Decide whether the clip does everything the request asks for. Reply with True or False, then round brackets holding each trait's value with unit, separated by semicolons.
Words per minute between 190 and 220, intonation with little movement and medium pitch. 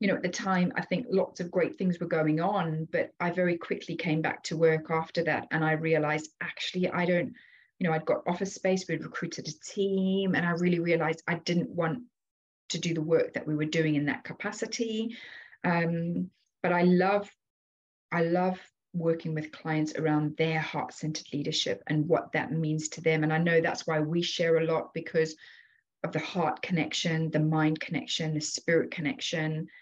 True (195 wpm; 2.2 semitones; 165 Hz)